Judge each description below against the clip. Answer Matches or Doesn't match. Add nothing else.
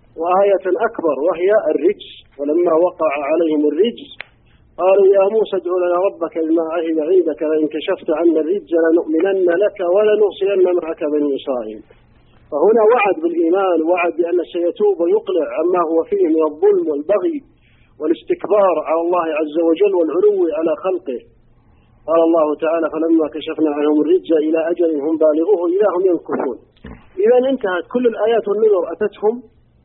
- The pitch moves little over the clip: Doesn't match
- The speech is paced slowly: Doesn't match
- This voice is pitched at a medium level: Matches